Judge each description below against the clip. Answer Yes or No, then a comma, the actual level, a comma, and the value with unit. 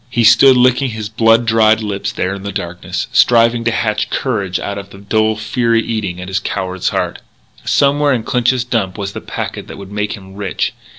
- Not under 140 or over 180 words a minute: No, average, 200 wpm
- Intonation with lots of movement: No, average, 2.8 semitones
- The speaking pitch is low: Yes, low, 110 Hz